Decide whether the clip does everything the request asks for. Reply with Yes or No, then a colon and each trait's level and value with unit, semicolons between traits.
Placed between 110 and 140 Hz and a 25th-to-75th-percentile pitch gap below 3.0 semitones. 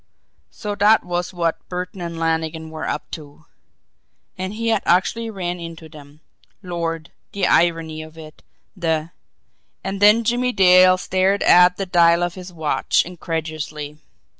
No: medium, 175 Hz; narrow, 2.6 semitones